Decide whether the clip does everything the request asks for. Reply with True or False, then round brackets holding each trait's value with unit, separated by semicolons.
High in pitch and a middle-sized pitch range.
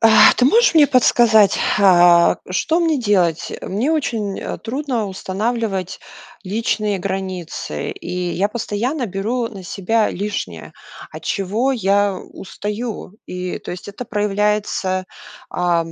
True (205 Hz; 3.6 semitones)